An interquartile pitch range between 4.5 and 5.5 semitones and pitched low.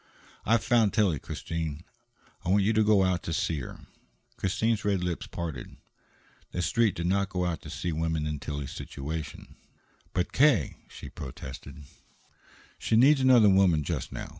Yes: average, 4.9 semitones; very low, 90 Hz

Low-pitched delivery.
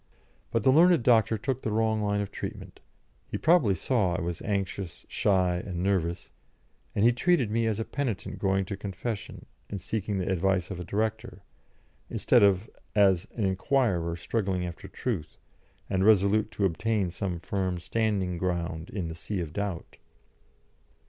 Yes: low, 100 Hz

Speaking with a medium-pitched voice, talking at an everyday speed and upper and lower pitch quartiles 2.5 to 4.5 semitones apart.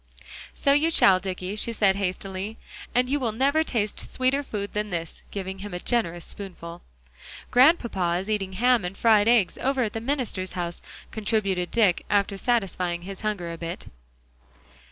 No: high, 205 Hz; average, 165 wpm; average, 4.2 semitones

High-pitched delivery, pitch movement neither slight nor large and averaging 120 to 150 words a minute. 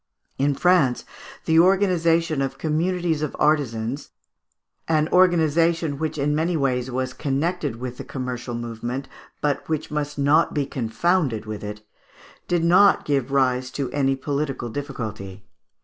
No: medium, 145 Hz; average, 4.3 semitones; slow, 135 wpm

